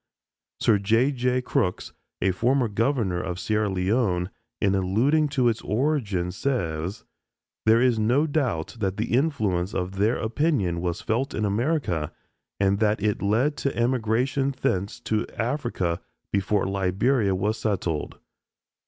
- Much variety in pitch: No, average, 5.0 semitones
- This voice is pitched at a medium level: No, low, 110 Hz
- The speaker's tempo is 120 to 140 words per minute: Yes, slow, 135 wpm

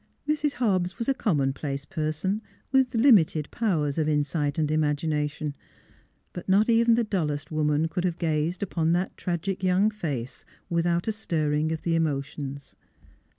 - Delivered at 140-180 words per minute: Yes, average, 150 wpm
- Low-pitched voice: No, medium, 165 Hz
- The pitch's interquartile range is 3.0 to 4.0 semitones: No, average, 4.7 semitones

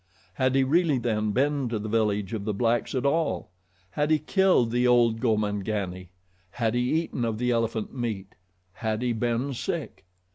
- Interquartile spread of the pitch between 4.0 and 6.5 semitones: No, average, 3.3 semitones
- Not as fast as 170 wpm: No, average, 175 wpm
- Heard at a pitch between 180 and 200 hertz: No, low, 115 Hz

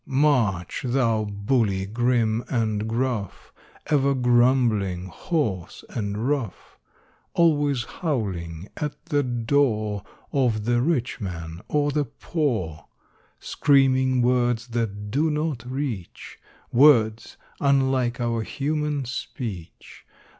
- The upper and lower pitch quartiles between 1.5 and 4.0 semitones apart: No, average, 4.5 semitones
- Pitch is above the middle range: No, low, 120 Hz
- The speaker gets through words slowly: Yes, slow, 100 wpm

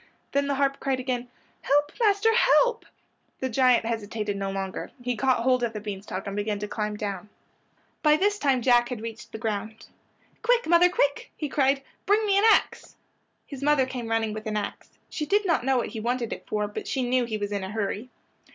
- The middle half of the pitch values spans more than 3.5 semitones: Yes, average, 4.8 semitones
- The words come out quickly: Yes, fast, 215 wpm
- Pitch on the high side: Yes, high, 245 Hz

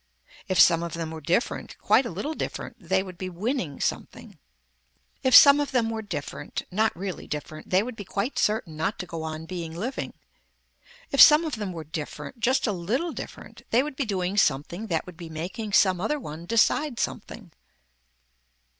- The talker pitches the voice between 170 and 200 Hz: Yes, high, 190 Hz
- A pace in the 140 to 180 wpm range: No, average, 190 wpm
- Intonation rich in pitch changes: Yes, wide, 5.8 semitones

